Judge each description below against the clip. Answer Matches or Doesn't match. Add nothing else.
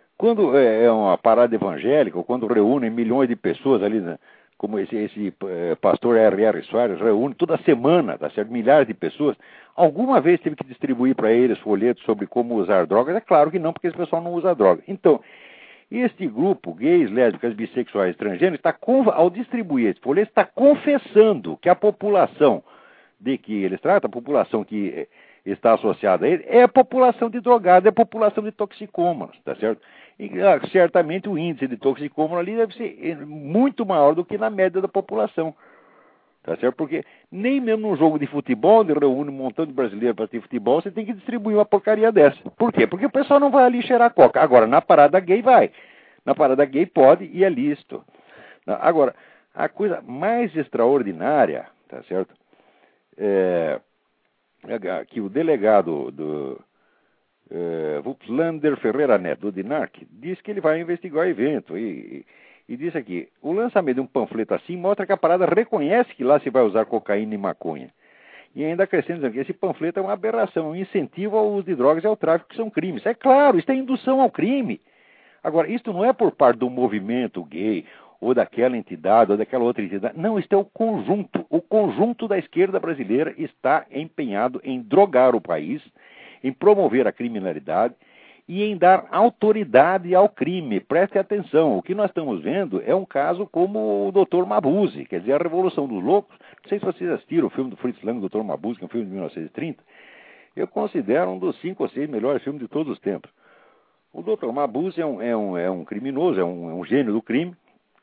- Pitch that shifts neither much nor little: Doesn't match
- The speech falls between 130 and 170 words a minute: Doesn't match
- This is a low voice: Doesn't match